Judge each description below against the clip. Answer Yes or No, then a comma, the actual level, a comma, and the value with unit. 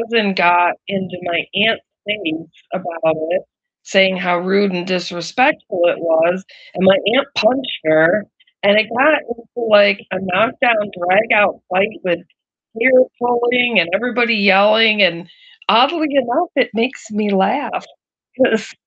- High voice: Yes, high, 200 Hz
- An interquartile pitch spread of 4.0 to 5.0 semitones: Yes, average, 4.6 semitones